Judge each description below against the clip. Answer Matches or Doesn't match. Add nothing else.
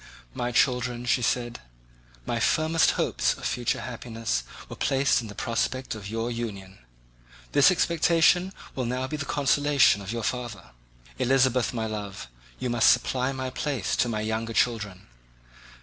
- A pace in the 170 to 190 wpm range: Doesn't match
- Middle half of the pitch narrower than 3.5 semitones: Matches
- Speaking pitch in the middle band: Doesn't match